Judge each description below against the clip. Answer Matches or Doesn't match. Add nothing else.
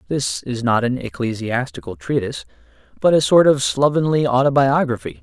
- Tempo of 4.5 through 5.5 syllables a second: Matches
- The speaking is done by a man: Matches